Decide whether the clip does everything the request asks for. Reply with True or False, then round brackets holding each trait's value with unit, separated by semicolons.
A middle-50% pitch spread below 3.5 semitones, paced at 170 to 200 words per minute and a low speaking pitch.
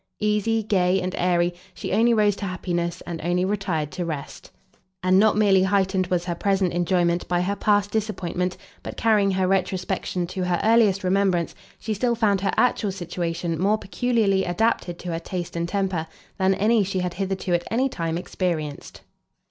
False (2.7 semitones; 175 wpm; 185 Hz)